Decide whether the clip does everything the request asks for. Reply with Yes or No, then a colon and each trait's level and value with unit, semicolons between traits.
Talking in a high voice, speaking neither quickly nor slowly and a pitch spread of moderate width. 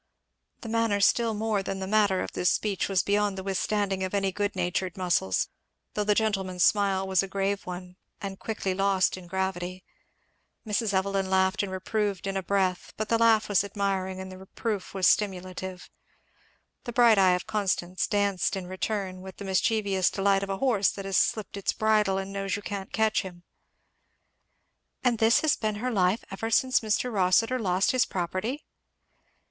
No: high, 195 Hz; average, 180 wpm; narrow, 2.0 semitones